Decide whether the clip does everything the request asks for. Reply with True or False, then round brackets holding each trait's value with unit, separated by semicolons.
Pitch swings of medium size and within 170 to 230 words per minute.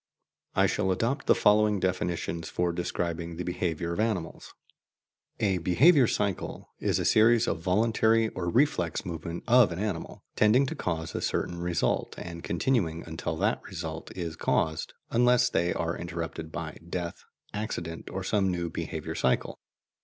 False (4.3 semitones; 155 wpm)